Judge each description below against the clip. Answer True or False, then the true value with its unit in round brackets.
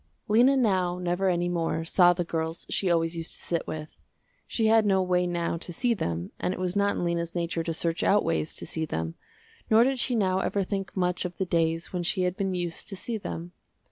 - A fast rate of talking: True (235 wpm)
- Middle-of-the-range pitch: True (180 Hz)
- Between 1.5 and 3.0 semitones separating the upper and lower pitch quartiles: True (2.7 semitones)